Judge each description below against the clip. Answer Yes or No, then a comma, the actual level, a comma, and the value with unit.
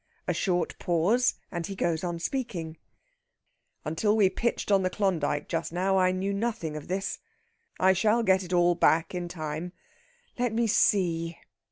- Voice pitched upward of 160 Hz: Yes, medium, 185 Hz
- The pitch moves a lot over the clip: No, average, 3.1 semitones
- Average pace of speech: Yes, average, 165 wpm